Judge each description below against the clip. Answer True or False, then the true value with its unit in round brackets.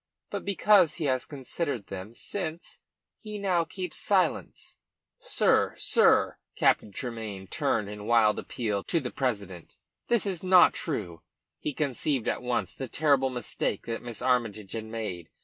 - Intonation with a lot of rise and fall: True (7.2 semitones)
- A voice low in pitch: True (125 Hz)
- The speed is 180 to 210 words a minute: False (150 wpm)